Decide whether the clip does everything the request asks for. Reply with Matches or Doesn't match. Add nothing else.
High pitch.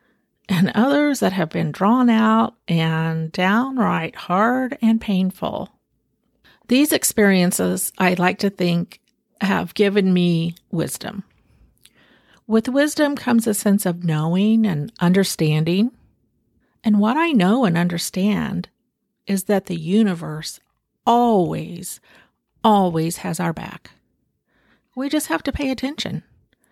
Matches